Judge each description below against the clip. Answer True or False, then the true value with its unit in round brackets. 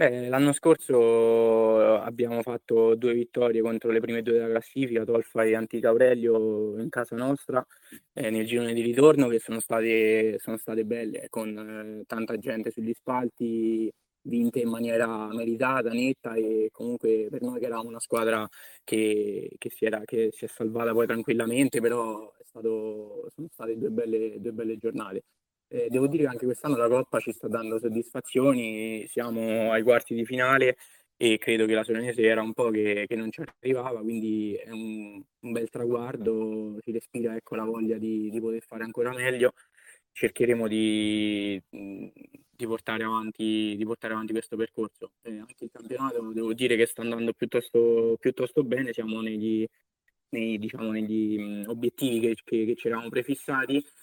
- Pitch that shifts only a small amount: True (1.5 semitones)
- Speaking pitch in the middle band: False (115 Hz)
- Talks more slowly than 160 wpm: False (165 wpm)